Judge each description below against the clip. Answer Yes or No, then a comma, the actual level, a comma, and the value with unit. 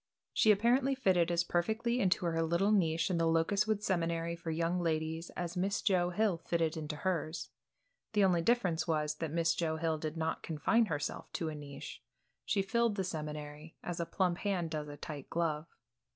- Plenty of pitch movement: No, average, 3.3 semitones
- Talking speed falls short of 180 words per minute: No, average, 185 wpm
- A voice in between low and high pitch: Yes, medium, 170 Hz